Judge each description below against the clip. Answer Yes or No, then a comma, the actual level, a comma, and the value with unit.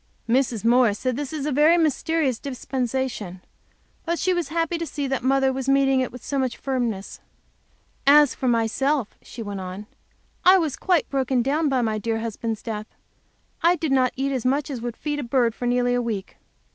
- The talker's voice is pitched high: Yes, very high, 260 Hz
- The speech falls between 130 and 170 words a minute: No, average, 200 wpm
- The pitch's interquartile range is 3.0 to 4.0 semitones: Yes, average, 3.6 semitones